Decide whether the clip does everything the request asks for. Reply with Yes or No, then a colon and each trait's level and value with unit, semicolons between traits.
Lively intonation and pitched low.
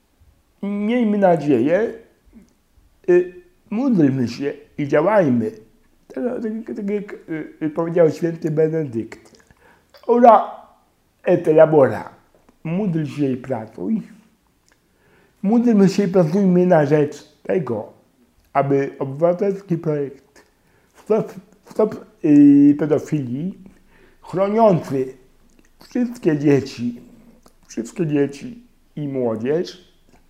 No: wide, 7.0 semitones; medium, 175 Hz